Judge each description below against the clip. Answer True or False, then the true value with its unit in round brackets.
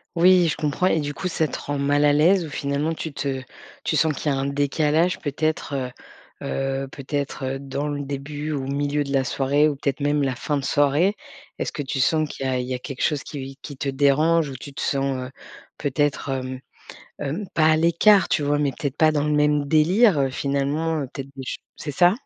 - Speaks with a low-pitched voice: False (145 Hz)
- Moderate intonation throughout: False (2.2 semitones)